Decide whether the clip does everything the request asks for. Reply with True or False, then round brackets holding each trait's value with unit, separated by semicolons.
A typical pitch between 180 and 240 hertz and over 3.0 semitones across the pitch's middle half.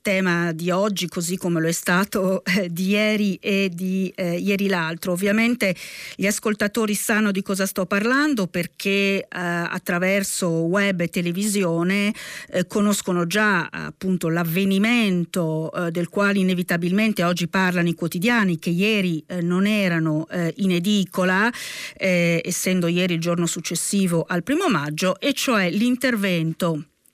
False (185 Hz; 2.6 semitones)